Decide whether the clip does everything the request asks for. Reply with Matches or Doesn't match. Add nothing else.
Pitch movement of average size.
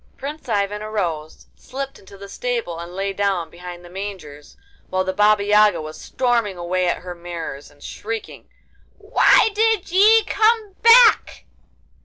Doesn't match